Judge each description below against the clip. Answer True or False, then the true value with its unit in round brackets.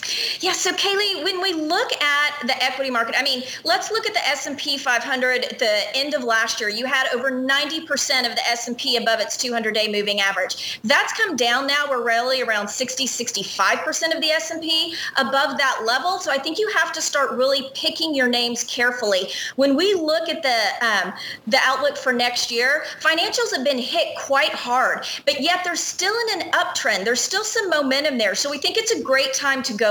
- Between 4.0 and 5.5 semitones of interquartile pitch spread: True (4.8 semitones)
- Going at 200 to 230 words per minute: True (205 wpm)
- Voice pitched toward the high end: True (280 Hz)